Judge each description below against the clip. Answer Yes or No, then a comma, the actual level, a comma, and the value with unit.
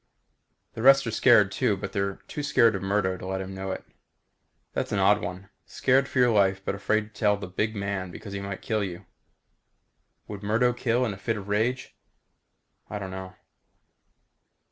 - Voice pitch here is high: No, low, 100 Hz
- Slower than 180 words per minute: No, average, 190 wpm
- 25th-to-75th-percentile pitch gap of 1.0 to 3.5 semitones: Yes, average, 2.9 semitones